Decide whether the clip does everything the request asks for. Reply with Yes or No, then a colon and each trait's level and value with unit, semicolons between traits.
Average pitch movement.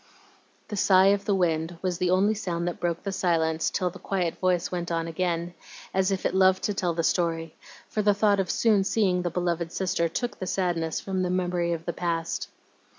No: narrow, 2.2 semitones